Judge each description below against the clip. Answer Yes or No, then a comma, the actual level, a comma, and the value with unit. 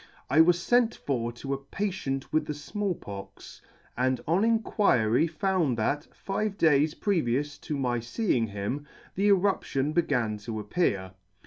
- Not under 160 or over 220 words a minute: No, average, 145 wpm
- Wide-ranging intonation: Yes, wide, 7.6 semitones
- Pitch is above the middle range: No, medium, 145 Hz